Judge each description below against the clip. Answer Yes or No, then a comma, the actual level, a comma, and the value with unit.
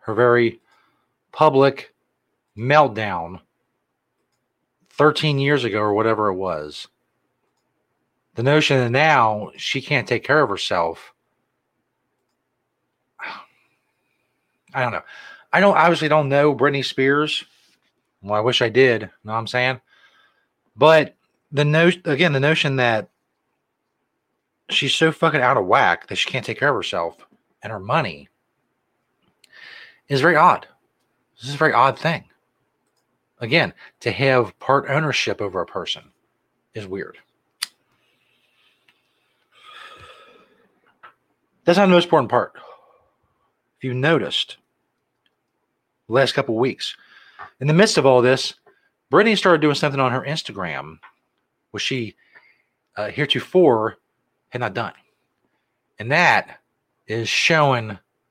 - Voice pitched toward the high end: No, medium, 140 Hz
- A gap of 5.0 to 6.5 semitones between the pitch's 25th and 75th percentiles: No, average, 4.2 semitones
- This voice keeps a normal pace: No, slow, 125 wpm